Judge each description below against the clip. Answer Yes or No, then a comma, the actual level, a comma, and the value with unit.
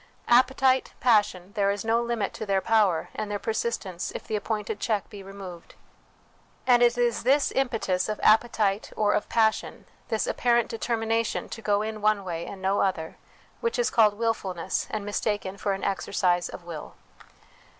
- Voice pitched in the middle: No, high, 215 Hz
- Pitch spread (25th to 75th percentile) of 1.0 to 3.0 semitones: Yes, average, 2.7 semitones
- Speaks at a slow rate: No, average, 170 wpm